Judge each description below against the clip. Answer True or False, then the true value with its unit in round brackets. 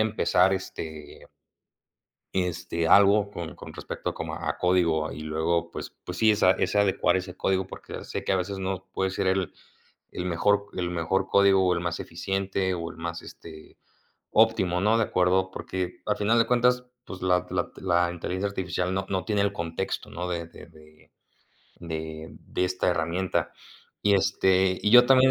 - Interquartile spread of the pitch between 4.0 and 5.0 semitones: False (2.4 semitones)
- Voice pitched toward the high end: False (95 Hz)